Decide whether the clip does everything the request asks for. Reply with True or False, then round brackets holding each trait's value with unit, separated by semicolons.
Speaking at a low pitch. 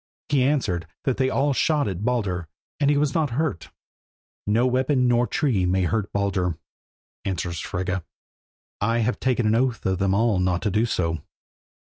True (110 Hz)